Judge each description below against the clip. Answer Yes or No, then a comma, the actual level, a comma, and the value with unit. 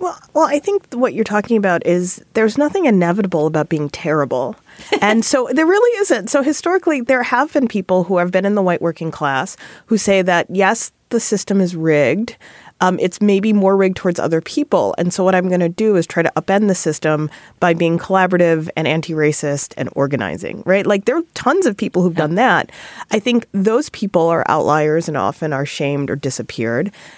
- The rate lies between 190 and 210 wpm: Yes, fast, 205 wpm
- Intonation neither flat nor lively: No, wide, 5.7 semitones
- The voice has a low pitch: No, medium, 185 Hz